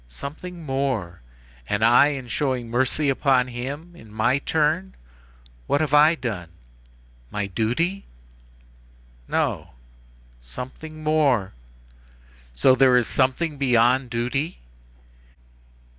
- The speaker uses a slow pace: Yes, slow, 100 wpm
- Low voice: Yes, low, 130 Hz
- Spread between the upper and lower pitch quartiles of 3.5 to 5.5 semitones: Yes, average, 4.8 semitones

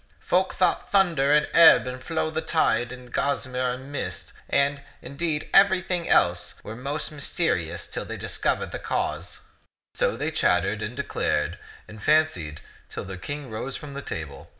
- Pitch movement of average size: No, wide, 6.5 semitones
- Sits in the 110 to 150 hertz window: Yes, low, 135 Hz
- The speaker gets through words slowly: No, average, 175 wpm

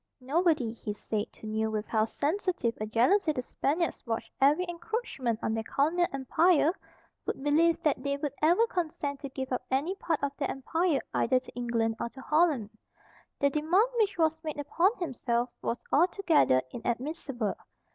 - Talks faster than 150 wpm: Yes, average, 165 wpm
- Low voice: No, very high, 280 Hz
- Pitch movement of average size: No, wide, 5.9 semitones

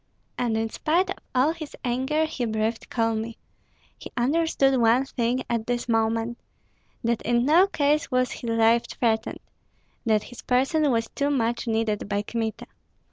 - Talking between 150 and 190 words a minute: Yes, average, 155 wpm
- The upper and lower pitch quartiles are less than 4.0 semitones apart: Yes, average, 3.3 semitones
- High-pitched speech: Yes, high, 240 Hz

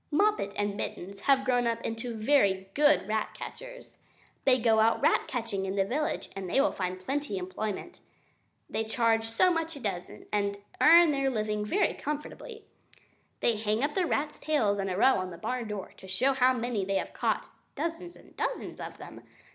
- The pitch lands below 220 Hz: No, high, 230 Hz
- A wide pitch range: Yes, wide, 6.1 semitones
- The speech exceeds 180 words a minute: Yes, average, 190 wpm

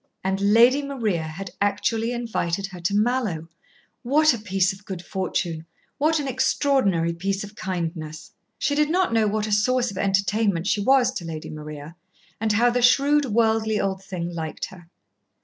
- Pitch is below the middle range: No, high, 205 Hz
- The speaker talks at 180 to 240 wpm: No, average, 170 wpm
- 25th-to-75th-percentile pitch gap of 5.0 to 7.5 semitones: Yes, average, 5.3 semitones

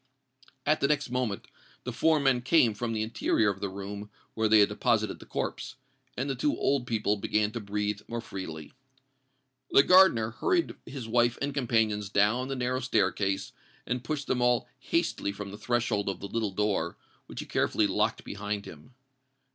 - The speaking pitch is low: Yes, low, 110 Hz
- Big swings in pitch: No, average, 3.6 semitones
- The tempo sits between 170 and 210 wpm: Yes, average, 180 wpm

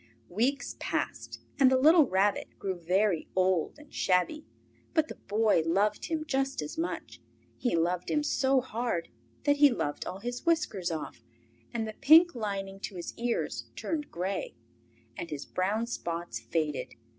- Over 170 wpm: No, average, 155 wpm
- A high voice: Yes, high, 215 Hz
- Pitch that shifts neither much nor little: No, wide, 7.1 semitones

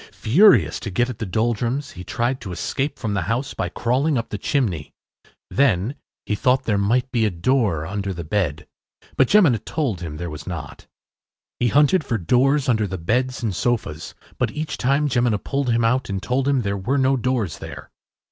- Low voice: Yes, low, 115 Hz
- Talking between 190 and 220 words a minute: Yes, average, 195 wpm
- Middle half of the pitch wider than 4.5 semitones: Yes, average, 5.3 semitones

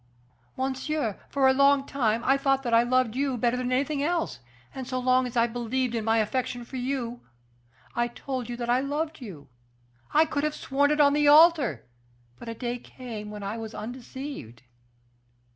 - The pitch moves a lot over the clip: No, average, 3.0 semitones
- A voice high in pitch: Yes, very high, 255 Hz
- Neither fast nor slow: Yes, average, 185 wpm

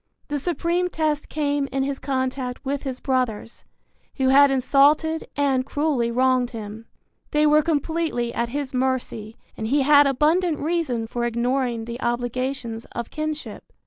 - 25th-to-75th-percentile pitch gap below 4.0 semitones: Yes, average, 3.5 semitones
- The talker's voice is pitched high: Yes, very high, 270 Hz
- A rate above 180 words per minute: No, average, 145 wpm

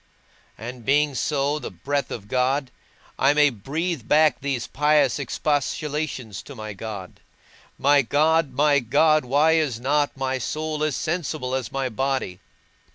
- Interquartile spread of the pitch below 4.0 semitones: Yes, average, 3.1 semitones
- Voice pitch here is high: No, medium, 140 Hz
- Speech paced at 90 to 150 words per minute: Yes, average, 145 wpm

